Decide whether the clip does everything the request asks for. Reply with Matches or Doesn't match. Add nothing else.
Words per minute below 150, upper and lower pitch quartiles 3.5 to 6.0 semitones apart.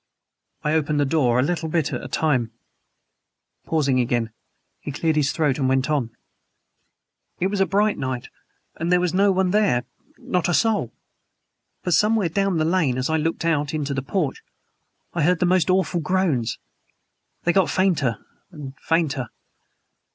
Doesn't match